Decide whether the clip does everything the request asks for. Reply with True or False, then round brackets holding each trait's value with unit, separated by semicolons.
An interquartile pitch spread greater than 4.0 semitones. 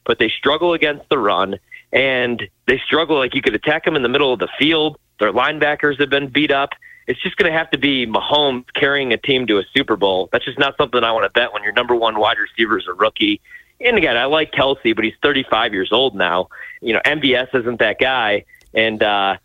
True (4.5 semitones)